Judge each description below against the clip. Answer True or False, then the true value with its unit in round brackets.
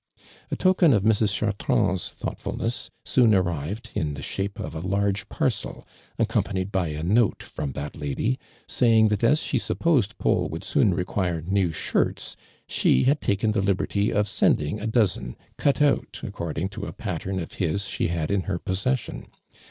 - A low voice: True (100 Hz)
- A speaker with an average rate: True (170 wpm)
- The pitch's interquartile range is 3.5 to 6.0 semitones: True (4.2 semitones)